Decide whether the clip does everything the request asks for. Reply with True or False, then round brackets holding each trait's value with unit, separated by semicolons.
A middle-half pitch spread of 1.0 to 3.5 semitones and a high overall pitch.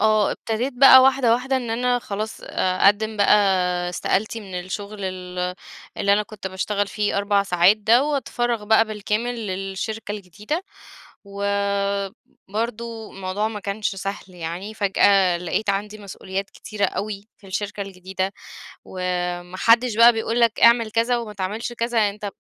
True (2.8 semitones; 210 Hz)